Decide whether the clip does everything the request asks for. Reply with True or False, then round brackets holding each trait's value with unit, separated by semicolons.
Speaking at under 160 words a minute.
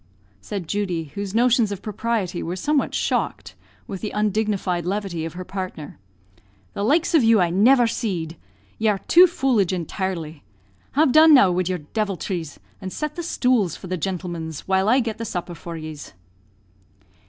False (165 wpm)